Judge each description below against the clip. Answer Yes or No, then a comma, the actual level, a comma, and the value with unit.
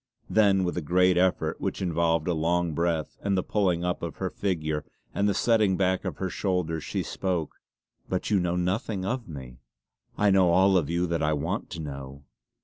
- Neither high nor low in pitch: No, very low, 90 Hz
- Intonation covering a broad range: No, average, 2.7 semitones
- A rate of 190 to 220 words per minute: Yes, average, 200 wpm